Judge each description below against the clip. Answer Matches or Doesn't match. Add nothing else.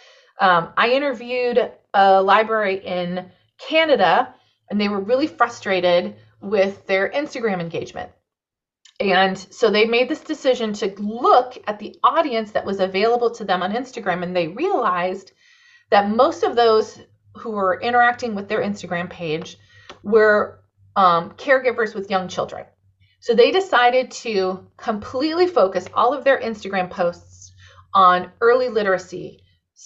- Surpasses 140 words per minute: Doesn't match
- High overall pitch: Matches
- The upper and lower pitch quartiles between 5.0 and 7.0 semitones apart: Matches